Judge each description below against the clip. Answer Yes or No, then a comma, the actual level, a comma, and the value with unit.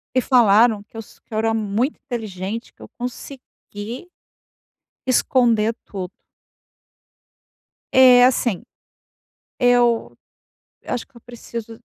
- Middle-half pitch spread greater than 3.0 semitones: No, narrow, 2.4 semitones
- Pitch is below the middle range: No, high, 235 Hz